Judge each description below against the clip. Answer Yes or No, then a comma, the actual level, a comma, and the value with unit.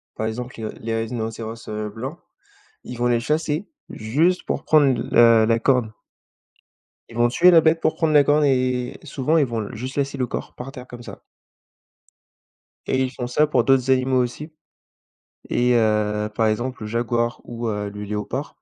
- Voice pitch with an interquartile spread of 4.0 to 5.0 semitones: No, average, 3.3 semitones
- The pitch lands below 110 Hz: No, low, 120 Hz